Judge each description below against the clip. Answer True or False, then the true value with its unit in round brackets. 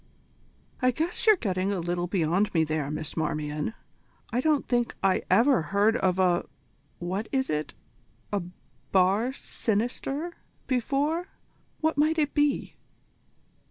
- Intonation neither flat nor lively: False (7.7 semitones)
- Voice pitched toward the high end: True (205 Hz)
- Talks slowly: True (130 wpm)